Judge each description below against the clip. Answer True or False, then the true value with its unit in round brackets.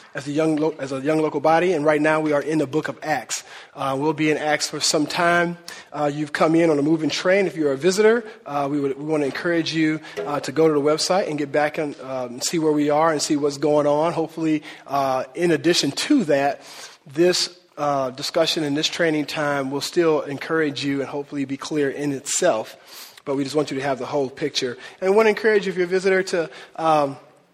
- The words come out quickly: True (240 wpm)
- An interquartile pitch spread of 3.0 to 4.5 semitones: False (2.5 semitones)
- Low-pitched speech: False (150 Hz)